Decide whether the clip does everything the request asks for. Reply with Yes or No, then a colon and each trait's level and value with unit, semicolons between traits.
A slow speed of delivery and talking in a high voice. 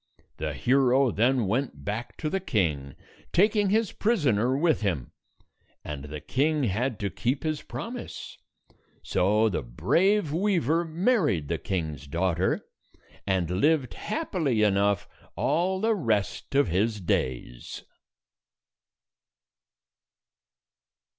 No: slow, 110 wpm; low, 120 Hz